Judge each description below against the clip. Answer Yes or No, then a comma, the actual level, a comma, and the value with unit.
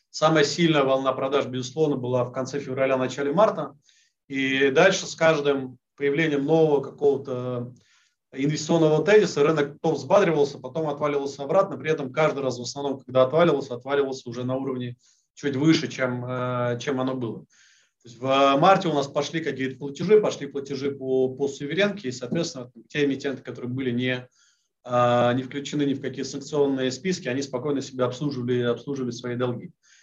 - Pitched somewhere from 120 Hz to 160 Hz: Yes, medium, 140 Hz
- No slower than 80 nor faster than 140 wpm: No, average, 150 wpm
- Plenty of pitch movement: No, narrow, 2.5 semitones